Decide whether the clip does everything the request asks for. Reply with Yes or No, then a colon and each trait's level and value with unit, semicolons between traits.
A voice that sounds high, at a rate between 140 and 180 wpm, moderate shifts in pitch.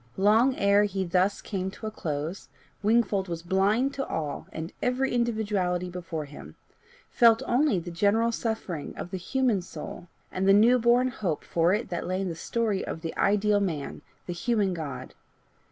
Yes: high, 195 Hz; average, 175 wpm; average, 4.5 semitones